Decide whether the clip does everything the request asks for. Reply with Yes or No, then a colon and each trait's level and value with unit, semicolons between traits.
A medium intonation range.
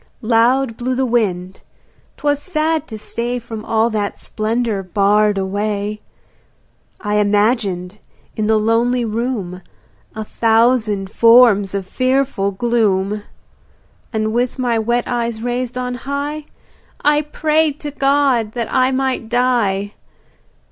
Yes: average, 3.4 semitones